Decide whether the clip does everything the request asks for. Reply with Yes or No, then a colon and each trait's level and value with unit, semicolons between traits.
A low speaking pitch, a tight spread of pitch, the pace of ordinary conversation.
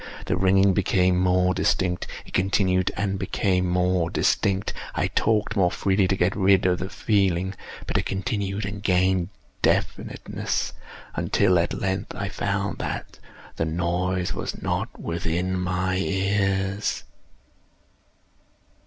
No: very low, 95 Hz; narrow, 1.3 semitones; slow, 120 wpm